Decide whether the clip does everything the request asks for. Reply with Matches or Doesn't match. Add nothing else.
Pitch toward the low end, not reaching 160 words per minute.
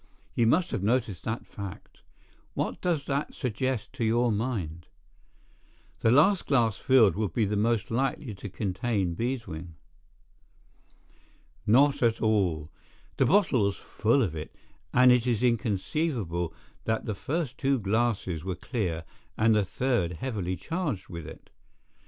Matches